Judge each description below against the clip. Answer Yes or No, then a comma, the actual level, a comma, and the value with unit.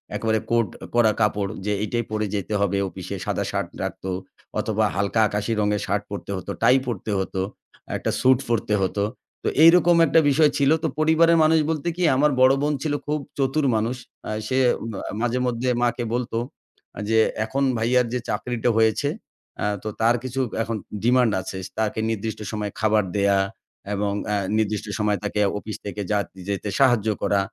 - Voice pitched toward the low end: Yes, low, 115 Hz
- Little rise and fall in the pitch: No, average, 3.8 semitones